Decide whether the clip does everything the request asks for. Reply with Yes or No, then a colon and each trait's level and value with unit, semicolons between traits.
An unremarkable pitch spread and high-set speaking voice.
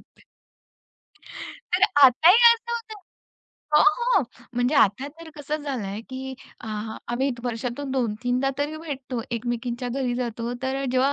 Yes: average, 3.1 semitones; very high, 260 Hz